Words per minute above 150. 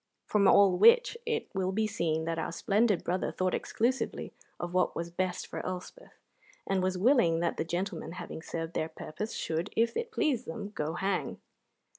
Yes: average, 180 wpm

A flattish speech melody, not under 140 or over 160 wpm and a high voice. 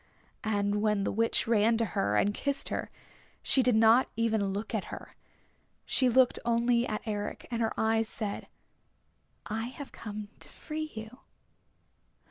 Yes: narrow, 2.2 semitones; average, 155 wpm; high, 225 Hz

